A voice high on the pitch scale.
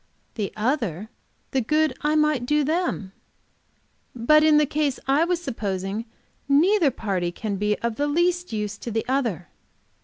Yes: very high, 265 Hz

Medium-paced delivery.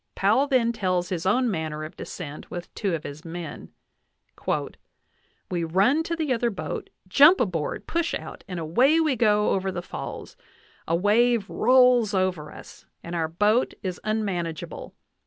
Yes: average, 160 wpm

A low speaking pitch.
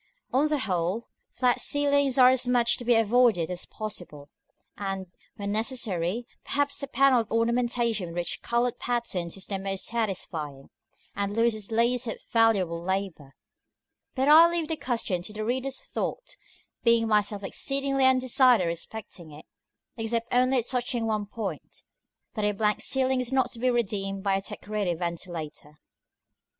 No: high, 225 Hz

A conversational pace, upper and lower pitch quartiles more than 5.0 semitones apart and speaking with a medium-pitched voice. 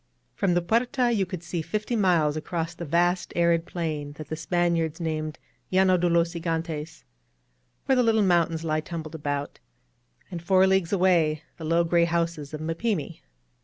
No: average, 170 wpm; narrow, 2.4 semitones; medium, 170 Hz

